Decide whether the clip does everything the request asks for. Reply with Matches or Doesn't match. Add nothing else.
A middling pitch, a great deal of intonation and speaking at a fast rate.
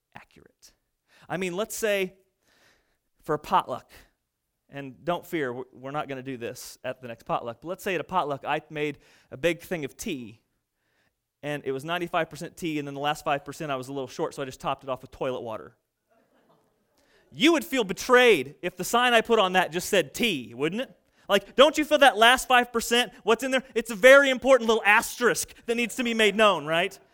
Matches